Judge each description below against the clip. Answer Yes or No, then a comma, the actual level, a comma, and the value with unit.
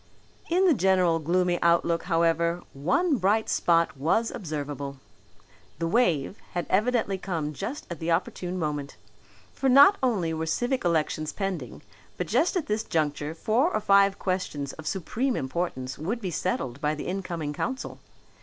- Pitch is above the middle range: No, medium, 175 Hz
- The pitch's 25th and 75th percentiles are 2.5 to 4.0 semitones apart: No, average, 5.2 semitones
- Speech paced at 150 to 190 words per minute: Yes, average, 155 wpm